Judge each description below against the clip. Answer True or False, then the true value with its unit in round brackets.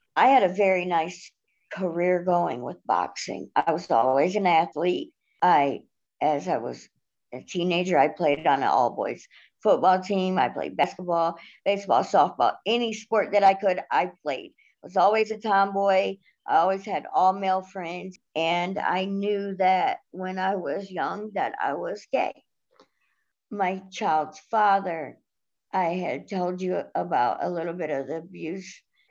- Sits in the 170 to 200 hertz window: True (190 Hz)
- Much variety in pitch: False (2.4 semitones)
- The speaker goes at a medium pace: True (155 wpm)